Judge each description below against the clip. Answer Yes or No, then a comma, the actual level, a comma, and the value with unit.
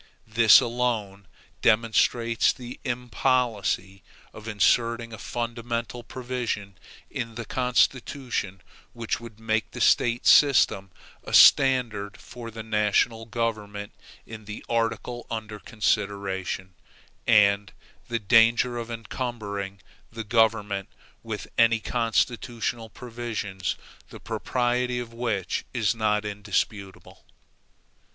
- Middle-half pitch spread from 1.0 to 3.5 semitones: Yes, narrow, 2.5 semitones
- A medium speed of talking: No, slow, 100 wpm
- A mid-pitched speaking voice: No, low, 115 Hz